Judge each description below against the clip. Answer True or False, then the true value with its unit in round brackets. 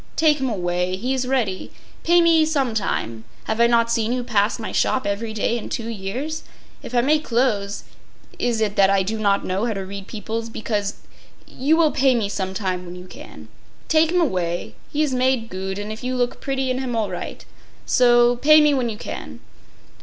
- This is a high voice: True (230 Hz)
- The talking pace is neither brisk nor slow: False (210 wpm)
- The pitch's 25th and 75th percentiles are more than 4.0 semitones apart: True (4.6 semitones)